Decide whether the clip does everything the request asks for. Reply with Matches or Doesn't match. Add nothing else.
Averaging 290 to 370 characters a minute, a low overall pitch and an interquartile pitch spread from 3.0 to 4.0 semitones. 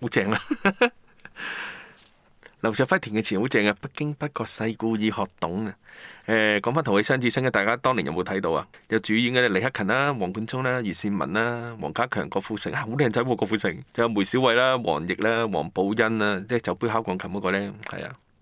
Matches